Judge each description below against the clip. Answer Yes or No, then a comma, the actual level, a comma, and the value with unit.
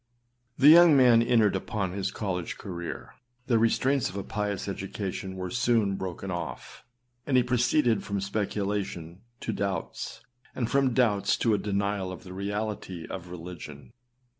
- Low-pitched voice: Yes, low, 100 Hz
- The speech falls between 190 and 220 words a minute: No, average, 150 wpm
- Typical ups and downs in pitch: Yes, average, 3.7 semitones